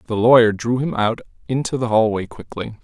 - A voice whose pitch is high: No, low, 115 Hz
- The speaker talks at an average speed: Yes, average, 190 wpm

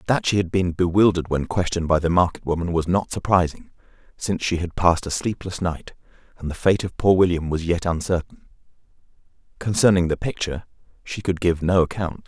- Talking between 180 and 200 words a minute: Yes, average, 185 wpm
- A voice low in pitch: Yes, very low, 90 Hz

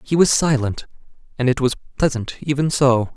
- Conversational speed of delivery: Yes, average, 170 wpm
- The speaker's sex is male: Yes, male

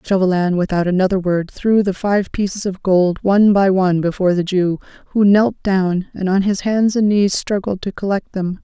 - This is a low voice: No, high, 190 Hz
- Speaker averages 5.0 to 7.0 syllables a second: Yes, 5.1 syllables/s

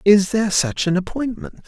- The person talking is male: Yes, male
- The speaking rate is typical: Yes, average, 180 wpm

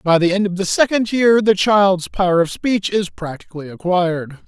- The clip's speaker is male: Yes, male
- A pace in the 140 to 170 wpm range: No, average, 200 wpm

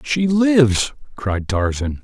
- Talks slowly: Yes, slow, 120 wpm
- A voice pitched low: Yes, low, 120 Hz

